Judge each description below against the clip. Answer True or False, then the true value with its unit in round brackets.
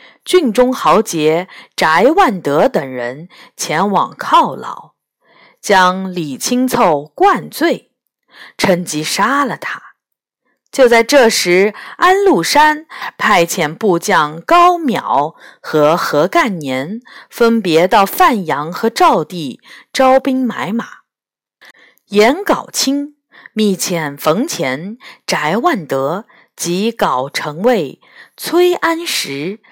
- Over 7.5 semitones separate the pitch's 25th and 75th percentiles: True (8.6 semitones)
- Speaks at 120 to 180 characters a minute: True (140 characters per minute)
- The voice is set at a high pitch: True (225 Hz)